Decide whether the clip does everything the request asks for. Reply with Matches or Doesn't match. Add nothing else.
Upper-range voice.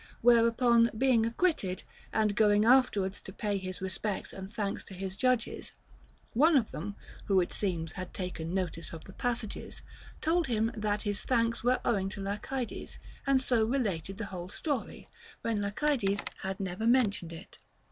Matches